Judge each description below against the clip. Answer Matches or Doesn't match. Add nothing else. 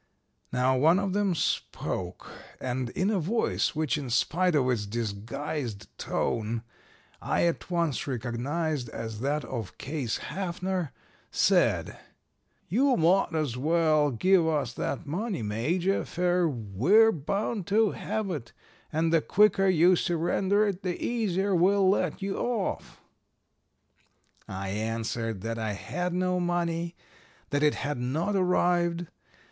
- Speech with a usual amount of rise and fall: Doesn't match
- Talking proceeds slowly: Matches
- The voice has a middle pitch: Matches